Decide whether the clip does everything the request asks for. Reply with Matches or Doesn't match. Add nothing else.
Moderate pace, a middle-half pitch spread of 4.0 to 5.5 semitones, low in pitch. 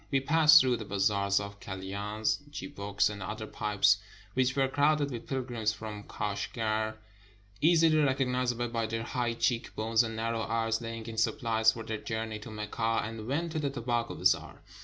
Doesn't match